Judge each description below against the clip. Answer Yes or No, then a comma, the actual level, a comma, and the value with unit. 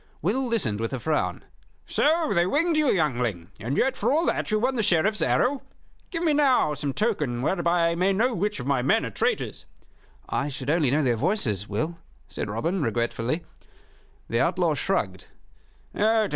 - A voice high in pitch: No, medium, 170 Hz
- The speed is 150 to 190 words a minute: Yes, average, 175 wpm